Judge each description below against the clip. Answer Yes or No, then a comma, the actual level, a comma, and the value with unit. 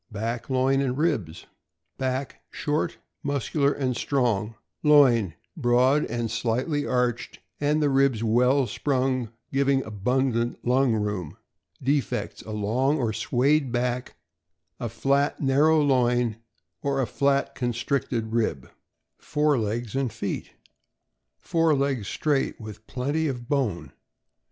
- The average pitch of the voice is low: Yes, low, 130 Hz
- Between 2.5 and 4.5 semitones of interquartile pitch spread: Yes, average, 3.3 semitones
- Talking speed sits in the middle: No, slow, 125 wpm